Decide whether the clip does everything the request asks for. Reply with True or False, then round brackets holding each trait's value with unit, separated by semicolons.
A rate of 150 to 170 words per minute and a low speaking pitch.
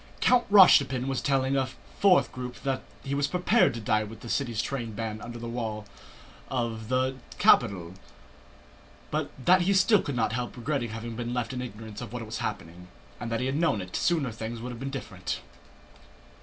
False (195 wpm; 125 Hz)